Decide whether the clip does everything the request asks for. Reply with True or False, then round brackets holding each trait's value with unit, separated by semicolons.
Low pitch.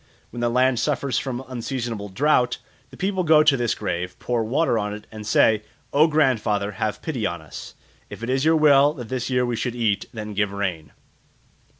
True (120 Hz)